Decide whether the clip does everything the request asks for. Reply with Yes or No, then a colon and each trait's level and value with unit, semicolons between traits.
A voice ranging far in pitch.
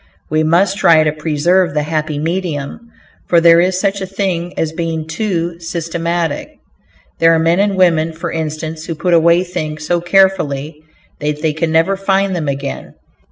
No: narrow, 2.6 semitones